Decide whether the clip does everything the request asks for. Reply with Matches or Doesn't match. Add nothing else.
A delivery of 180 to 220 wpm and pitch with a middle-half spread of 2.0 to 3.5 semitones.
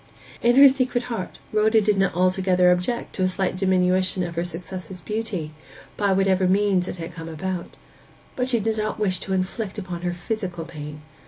Matches